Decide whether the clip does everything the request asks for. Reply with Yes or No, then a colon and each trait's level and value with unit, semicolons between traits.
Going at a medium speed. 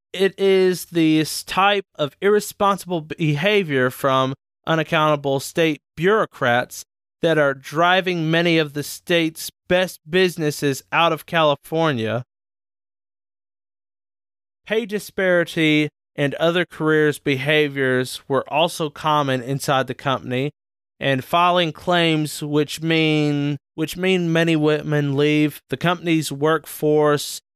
No: slow, 105 wpm